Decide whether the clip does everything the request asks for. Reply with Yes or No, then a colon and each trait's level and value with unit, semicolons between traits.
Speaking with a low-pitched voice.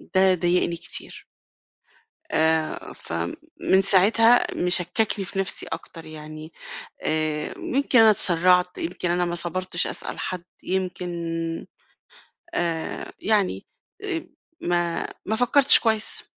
No: medium, 180 Hz